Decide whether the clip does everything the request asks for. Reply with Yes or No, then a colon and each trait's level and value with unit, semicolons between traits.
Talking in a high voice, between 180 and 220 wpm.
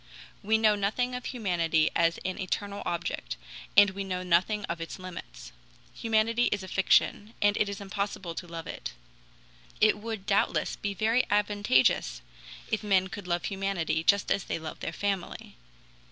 No: high, 195 Hz; average, 165 wpm